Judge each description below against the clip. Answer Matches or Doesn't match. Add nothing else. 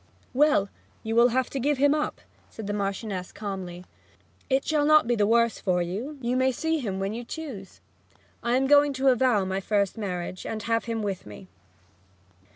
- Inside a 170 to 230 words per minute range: Matches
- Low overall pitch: Doesn't match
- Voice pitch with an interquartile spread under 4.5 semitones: Doesn't match